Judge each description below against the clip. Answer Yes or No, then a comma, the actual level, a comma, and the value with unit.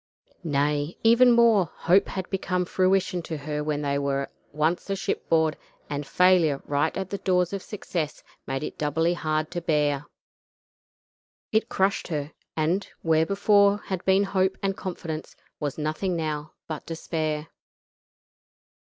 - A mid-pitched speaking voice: Yes, medium, 165 Hz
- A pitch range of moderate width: Yes, average, 4.0 semitones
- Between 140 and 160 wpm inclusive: Yes, average, 145 wpm